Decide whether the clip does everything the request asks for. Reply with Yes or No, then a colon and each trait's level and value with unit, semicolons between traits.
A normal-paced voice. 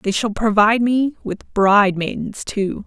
Yes: average, 170 wpm